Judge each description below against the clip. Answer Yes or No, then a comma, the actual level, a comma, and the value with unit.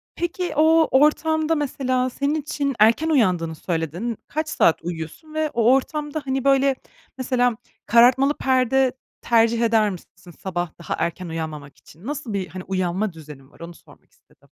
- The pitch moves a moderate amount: No, wide, 8.1 semitones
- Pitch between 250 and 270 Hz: No, high, 240 Hz